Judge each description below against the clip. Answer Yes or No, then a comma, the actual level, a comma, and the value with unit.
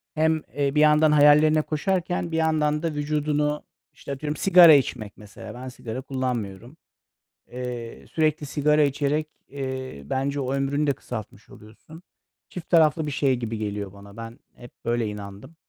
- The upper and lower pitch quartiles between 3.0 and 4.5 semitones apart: Yes, average, 4.2 semitones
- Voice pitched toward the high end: No, medium, 140 Hz